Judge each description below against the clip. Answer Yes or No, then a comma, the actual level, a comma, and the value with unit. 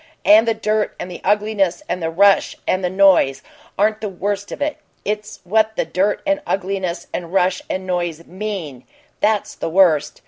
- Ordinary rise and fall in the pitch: Yes, average, 3.0 semitones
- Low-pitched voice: No, high, 195 Hz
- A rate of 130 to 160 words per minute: No, average, 180 wpm